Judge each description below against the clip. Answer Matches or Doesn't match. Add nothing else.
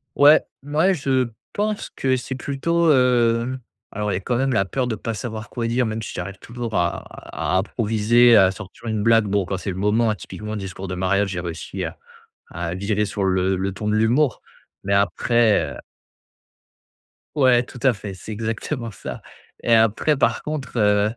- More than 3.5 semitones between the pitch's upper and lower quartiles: Matches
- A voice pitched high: Doesn't match